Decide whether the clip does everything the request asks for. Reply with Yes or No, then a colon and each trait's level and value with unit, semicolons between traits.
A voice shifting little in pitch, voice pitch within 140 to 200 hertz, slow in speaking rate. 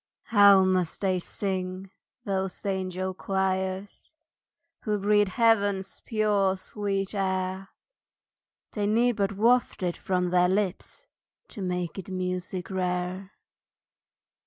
Yes: narrow, 1.6 semitones; high, 190 Hz; slow, 110 wpm